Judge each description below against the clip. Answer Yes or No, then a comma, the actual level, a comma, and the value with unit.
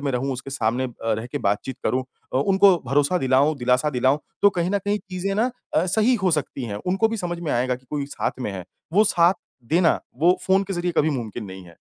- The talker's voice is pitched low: No, medium, 145 Hz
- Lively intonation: Yes, wide, 6.5 semitones